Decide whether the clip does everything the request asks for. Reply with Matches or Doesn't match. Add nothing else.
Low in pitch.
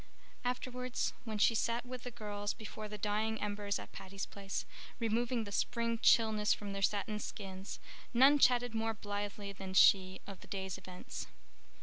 Doesn't match